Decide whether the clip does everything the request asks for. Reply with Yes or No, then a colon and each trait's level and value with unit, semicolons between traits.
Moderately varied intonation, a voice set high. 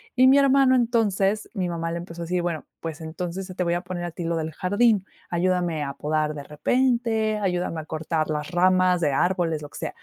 No: average, 4.0 semitones; medium, 175 Hz